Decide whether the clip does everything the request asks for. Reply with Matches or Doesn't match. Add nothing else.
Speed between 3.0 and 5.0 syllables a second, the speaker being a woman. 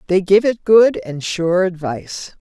Matches